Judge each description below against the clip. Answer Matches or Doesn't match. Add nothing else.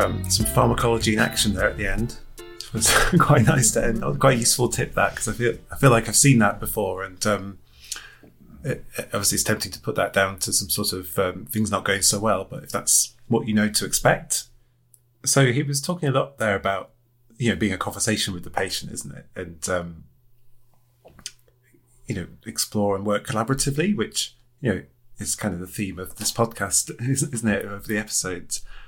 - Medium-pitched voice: Doesn't match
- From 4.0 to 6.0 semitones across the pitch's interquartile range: Doesn't match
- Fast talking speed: Matches